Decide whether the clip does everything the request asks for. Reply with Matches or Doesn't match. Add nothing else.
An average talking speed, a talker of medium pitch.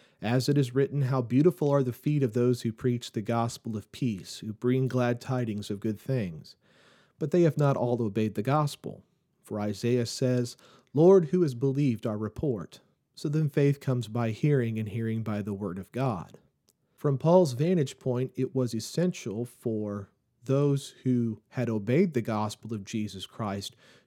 Doesn't match